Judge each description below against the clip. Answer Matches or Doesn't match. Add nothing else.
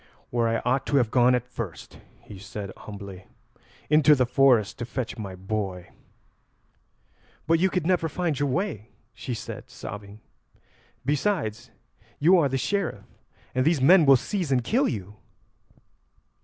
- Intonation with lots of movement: Matches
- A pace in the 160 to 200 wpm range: Doesn't match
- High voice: Doesn't match